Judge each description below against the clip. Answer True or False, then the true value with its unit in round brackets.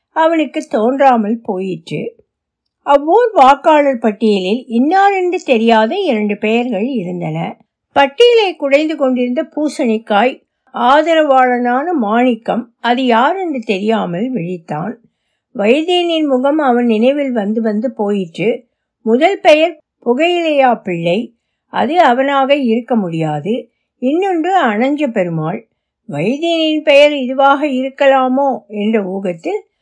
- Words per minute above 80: True (95 wpm)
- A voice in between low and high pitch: False (255 Hz)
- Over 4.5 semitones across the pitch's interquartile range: True (5.2 semitones)